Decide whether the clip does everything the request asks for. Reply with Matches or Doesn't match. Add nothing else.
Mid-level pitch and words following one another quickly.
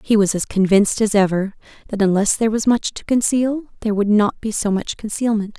Doesn't match